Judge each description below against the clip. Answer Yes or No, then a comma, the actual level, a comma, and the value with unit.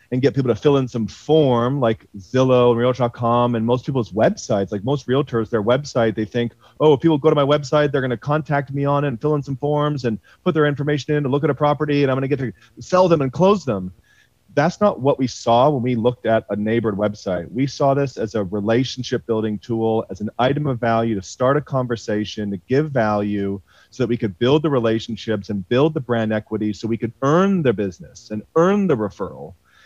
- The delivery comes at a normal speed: No, fast, 230 wpm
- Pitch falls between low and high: No, low, 125 Hz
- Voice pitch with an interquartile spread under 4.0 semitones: No, average, 4.3 semitones